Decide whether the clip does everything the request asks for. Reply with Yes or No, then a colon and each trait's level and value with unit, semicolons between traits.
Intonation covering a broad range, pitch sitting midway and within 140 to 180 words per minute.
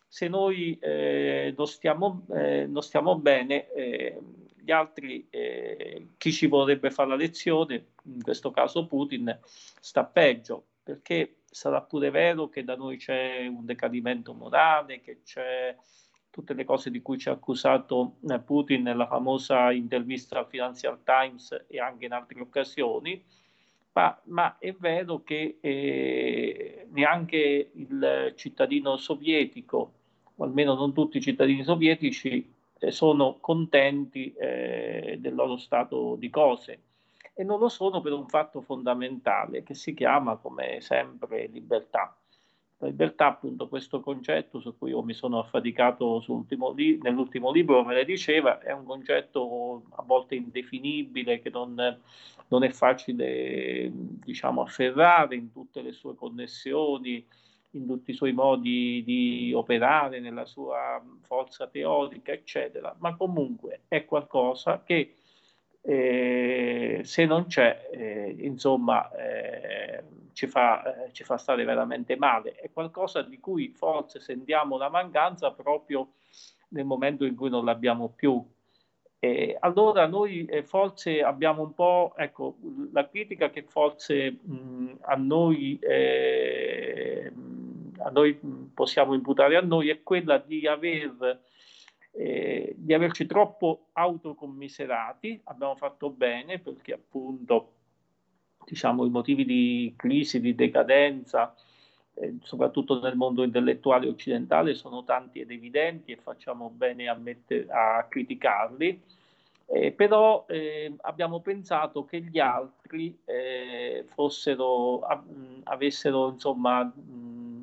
No: wide, 6.6 semitones; medium, 145 Hz; average, 130 wpm